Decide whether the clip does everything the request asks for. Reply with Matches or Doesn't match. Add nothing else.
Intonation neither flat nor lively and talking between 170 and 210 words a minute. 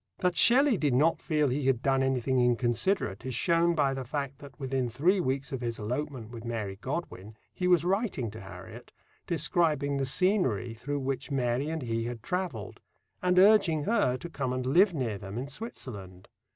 Doesn't match